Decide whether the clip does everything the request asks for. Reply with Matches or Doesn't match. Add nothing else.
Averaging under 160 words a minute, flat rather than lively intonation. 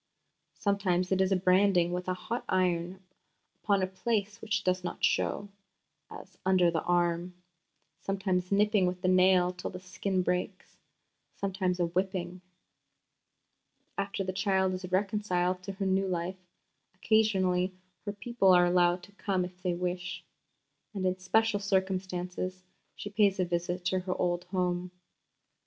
Matches